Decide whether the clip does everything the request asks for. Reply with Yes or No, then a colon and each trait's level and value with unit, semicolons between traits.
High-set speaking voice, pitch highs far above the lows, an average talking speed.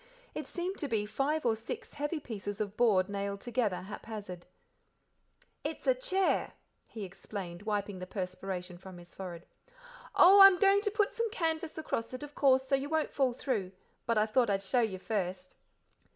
Yes: high, 220 Hz; wide, 7.3 semitones; average, 180 wpm